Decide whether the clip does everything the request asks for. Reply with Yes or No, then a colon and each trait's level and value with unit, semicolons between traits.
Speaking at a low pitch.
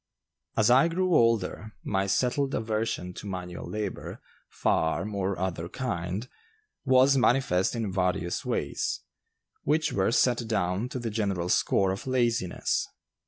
Yes: low, 105 Hz